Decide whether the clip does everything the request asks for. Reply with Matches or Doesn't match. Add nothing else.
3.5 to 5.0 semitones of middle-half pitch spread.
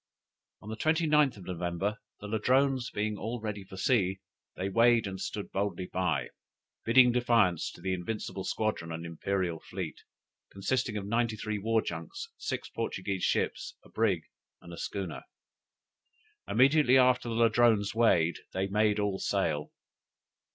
Matches